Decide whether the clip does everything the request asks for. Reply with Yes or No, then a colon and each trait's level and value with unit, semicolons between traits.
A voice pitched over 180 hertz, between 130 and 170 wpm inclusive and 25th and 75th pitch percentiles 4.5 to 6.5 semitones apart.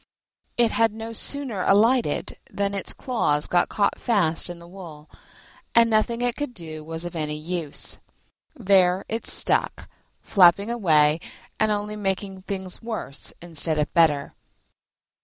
Yes: high, 190 Hz; average, 140 wpm; average, 5.2 semitones